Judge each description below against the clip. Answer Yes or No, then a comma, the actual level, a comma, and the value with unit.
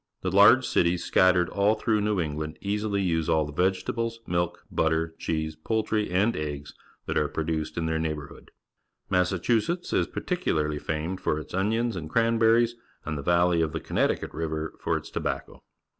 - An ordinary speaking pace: Yes, average, 170 wpm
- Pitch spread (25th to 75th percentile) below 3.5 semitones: No, average, 5.1 semitones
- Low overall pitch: Yes, very low, 90 Hz